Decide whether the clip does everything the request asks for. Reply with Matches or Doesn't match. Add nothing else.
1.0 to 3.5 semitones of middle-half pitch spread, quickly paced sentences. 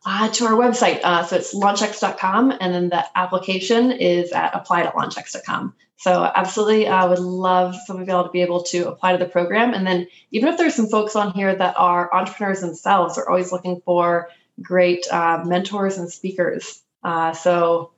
Doesn't match